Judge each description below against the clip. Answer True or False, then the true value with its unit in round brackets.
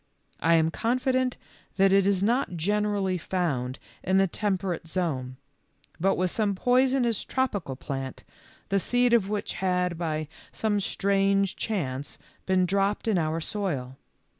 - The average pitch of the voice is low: False (190 Hz)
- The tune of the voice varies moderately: True (4.1 semitones)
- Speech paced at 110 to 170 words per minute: True (140 wpm)